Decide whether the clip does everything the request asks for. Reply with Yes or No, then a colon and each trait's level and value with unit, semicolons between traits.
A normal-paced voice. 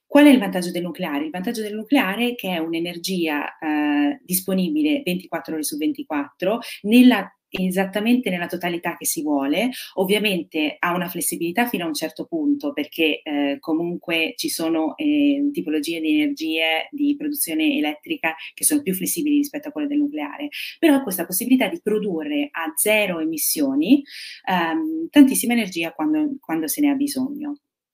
Yes: average, 160 wpm